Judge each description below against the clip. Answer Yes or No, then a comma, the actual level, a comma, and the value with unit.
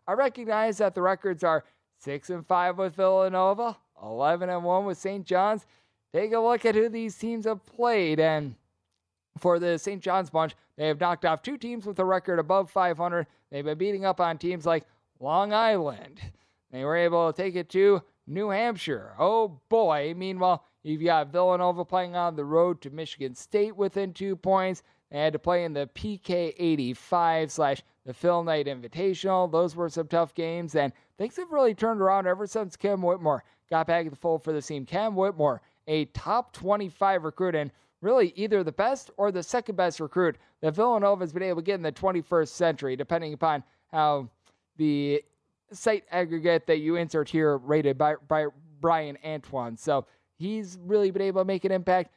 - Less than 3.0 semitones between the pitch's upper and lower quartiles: No, average, 4.0 semitones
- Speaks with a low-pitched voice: No, medium, 175 Hz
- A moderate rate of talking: Yes, average, 185 wpm